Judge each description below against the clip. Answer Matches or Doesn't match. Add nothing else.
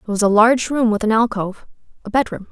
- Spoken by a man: Doesn't match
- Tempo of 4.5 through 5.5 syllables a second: Doesn't match